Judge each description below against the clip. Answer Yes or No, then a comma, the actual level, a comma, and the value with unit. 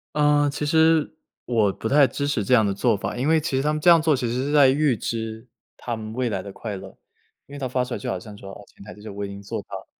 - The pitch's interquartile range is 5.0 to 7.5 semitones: Yes, wide, 5.5 semitones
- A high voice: No, low, 125 Hz